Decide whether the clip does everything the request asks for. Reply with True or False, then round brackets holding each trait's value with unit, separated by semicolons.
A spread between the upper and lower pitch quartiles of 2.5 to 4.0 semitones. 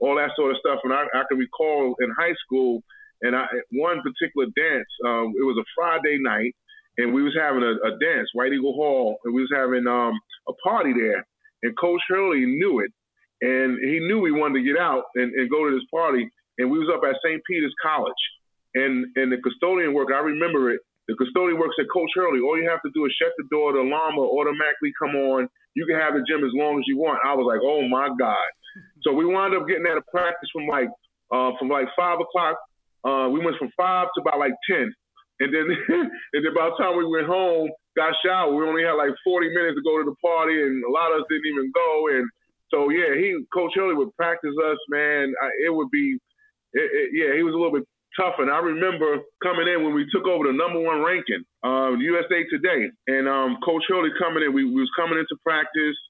False (4.8 semitones)